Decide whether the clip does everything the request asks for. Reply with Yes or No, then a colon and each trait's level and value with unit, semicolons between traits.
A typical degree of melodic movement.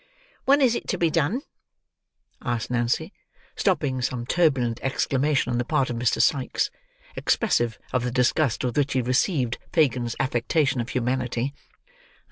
Yes: average, 3.7 semitones